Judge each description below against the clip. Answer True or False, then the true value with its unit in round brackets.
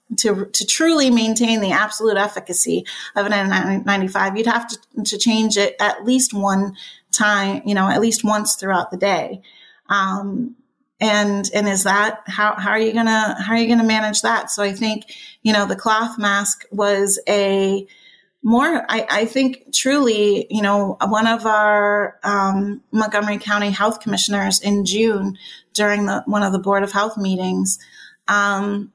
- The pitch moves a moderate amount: False (1.9 semitones)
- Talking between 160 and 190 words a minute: True (170 wpm)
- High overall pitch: True (210 Hz)